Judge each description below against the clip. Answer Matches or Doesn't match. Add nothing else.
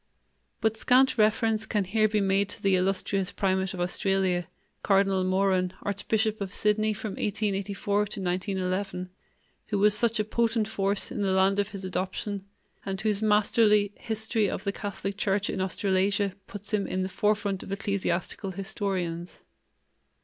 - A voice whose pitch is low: Doesn't match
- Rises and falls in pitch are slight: Matches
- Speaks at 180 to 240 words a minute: Doesn't match